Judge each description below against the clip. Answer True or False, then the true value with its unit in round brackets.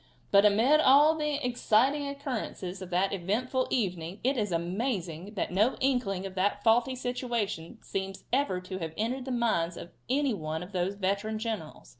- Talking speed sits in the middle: True (170 wpm)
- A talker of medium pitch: False (210 Hz)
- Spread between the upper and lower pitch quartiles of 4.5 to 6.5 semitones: True (5.5 semitones)